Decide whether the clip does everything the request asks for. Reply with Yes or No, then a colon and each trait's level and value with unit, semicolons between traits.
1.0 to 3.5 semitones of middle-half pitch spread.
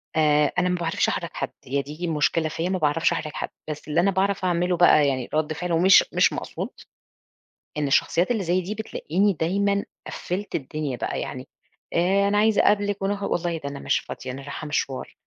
No: average, 4.3 semitones